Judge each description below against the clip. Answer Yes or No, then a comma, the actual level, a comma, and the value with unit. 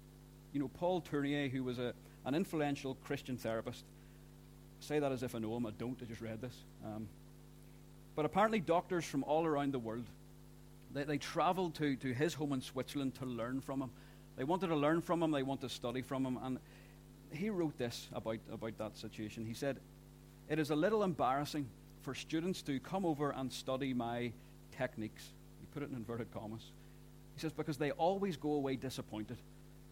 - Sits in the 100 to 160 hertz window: Yes, low, 135 Hz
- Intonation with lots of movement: No, average, 3.7 semitones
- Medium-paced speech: Yes, average, 195 wpm